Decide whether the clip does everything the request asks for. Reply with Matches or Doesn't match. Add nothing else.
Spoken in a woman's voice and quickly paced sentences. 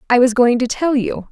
Matches